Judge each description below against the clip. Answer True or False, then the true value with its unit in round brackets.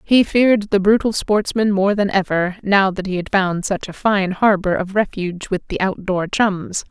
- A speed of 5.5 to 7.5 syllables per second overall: False (4.6 syllables/s)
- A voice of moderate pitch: False (195 Hz)